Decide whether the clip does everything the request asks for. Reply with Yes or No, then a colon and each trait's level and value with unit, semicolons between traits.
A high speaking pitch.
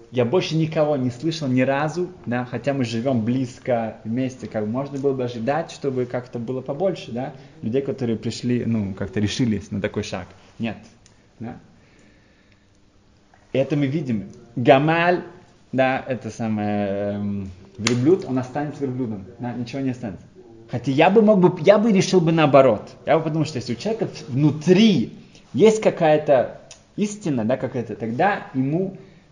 No: low, 125 Hz